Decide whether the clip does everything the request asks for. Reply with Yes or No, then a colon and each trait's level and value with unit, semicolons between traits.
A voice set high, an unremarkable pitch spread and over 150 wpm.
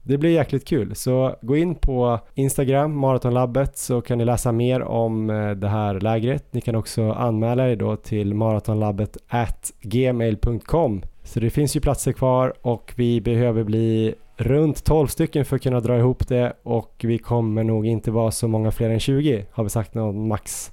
No: low, 120 Hz; average, 3.0 semitones; average, 180 wpm